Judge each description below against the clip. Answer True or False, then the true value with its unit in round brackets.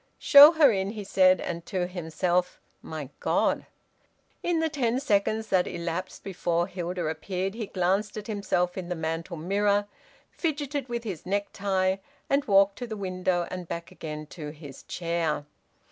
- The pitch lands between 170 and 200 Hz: True (185 Hz)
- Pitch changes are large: False (3.3 semitones)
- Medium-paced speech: True (160 wpm)